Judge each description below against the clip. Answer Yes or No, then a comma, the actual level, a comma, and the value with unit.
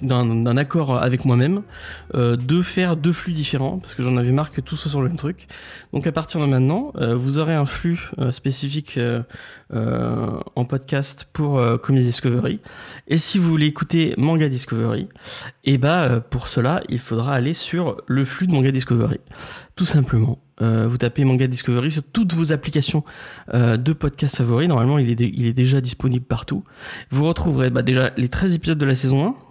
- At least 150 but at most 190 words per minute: No, average, 200 wpm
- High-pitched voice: No, low, 135 Hz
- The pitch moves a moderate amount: Yes, average, 4.2 semitones